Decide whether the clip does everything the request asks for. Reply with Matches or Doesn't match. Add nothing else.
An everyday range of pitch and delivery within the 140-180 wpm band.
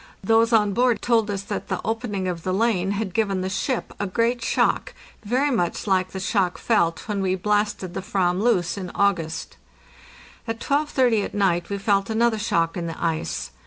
Doesn't match